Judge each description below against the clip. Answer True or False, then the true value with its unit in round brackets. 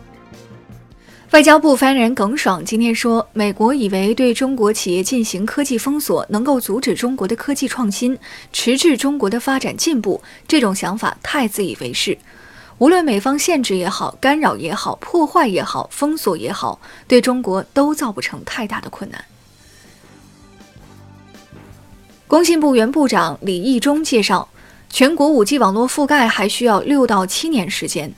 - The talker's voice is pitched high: True (245 Hz)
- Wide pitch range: True (5.7 semitones)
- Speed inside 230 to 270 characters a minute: True (245 characters per minute)